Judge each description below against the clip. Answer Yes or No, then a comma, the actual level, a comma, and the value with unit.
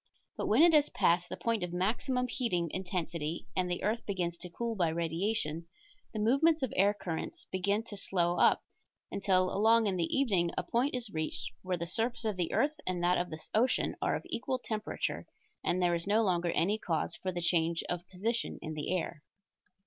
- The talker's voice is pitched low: No, medium, 185 Hz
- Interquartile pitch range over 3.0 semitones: Yes, average, 4.7 semitones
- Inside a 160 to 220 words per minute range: Yes, average, 200 wpm